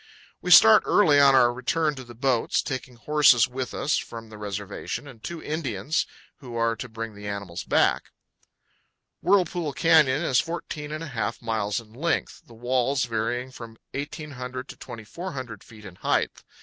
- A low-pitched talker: Yes, low, 125 Hz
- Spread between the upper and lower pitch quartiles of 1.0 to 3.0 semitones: No, average, 4.6 semitones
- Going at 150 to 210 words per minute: Yes, average, 160 wpm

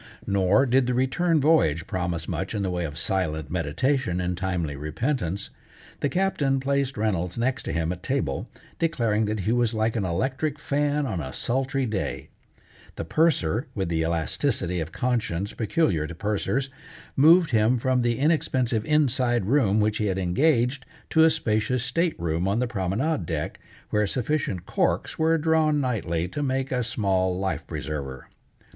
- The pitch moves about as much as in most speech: No, wide, 7.0 semitones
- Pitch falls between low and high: No, low, 110 Hz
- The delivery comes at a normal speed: Yes, average, 165 wpm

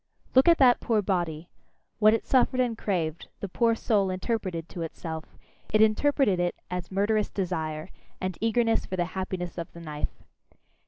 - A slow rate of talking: No, average, 165 wpm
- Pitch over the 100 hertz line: Yes, high, 190 Hz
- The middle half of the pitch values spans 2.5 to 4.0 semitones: No, average, 4.7 semitones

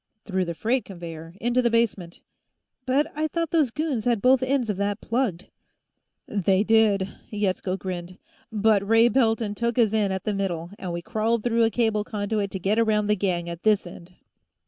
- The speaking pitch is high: Yes, high, 210 Hz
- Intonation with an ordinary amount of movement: Yes, average, 3.6 semitones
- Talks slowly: No, average, 190 wpm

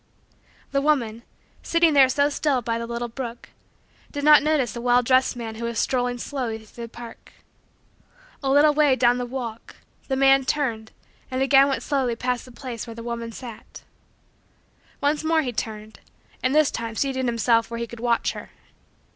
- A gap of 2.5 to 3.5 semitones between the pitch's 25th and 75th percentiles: Yes, average, 2.8 semitones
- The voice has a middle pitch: No, high, 245 Hz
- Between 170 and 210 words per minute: Yes, average, 180 wpm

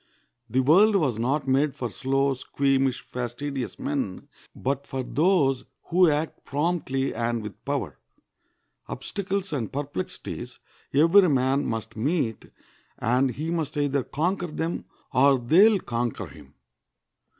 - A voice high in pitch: No, medium, 140 Hz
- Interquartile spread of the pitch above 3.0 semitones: Yes, average, 4.2 semitones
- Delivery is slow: Yes, slow, 130 wpm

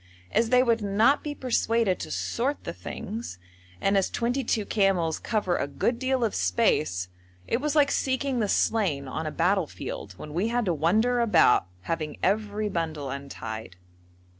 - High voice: Yes, high, 205 Hz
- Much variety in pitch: Yes, wide, 6.9 semitones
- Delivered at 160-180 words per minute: Yes, average, 165 wpm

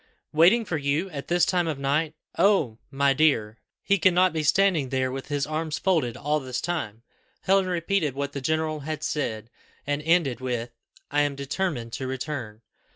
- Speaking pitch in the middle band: Yes, medium, 150 Hz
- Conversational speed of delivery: Yes, average, 175 wpm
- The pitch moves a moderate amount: Yes, average, 4.1 semitones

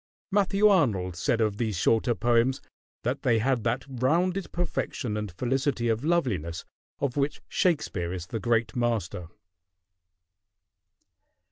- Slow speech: Yes, slow, 125 wpm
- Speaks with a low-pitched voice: Yes, low, 120 Hz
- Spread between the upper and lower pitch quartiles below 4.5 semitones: No, average, 4.9 semitones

